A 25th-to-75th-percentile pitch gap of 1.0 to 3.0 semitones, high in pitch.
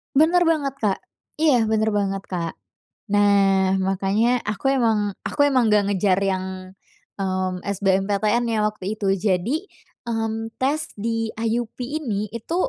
No: average, 3.6 semitones; high, 215 Hz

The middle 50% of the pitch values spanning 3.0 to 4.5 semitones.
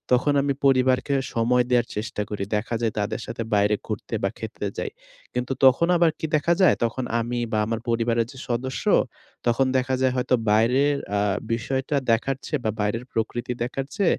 No: narrow, 2.6 semitones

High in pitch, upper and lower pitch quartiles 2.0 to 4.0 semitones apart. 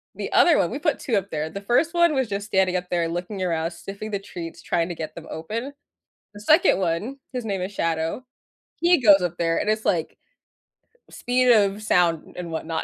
No: high, 195 Hz; average, 4.5 semitones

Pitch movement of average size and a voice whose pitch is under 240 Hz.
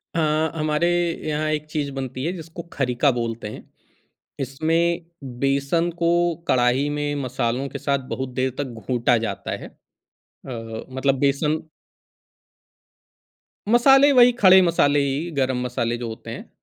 Yes: average, 4.0 semitones; medium, 140 Hz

